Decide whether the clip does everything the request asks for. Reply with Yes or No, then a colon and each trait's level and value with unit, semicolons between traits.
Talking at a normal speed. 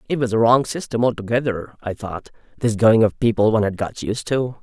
No: fast, 220 wpm